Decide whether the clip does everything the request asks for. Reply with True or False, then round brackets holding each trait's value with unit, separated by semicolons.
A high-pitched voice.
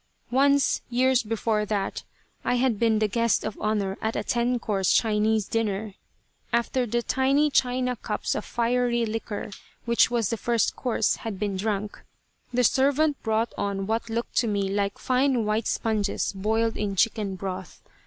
True (225 Hz)